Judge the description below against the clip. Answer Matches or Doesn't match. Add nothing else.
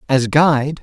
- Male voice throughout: Matches